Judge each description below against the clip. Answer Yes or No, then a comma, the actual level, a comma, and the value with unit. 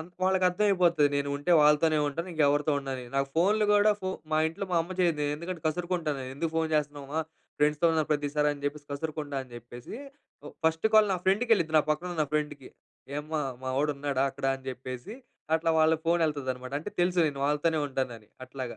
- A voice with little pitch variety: No, average, 3.2 semitones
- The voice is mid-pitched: Yes, medium, 150 Hz